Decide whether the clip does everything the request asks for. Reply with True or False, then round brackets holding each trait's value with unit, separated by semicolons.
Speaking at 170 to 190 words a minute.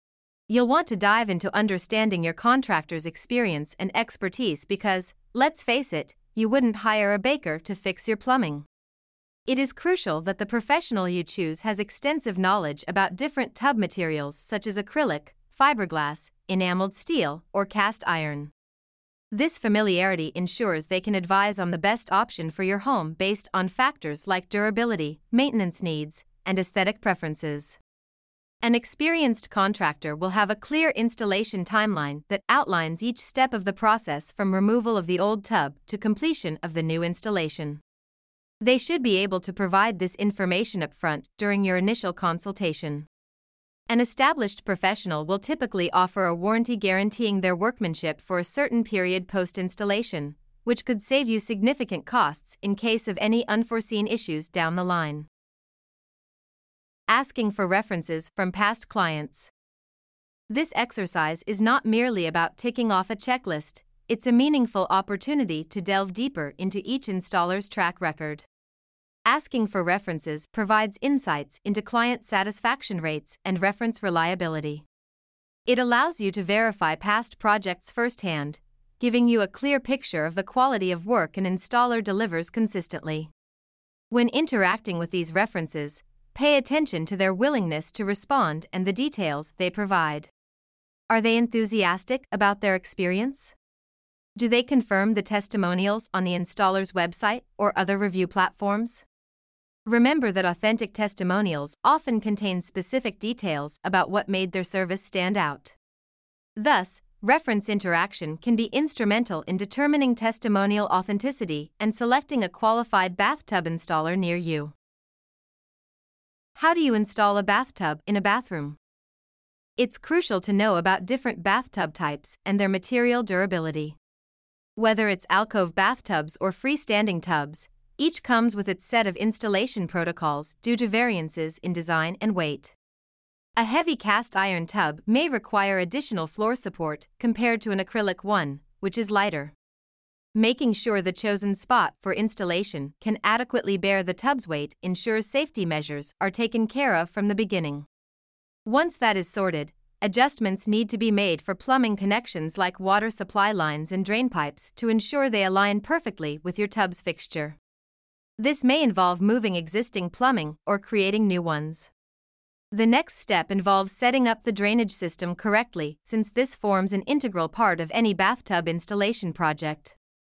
False (145 wpm)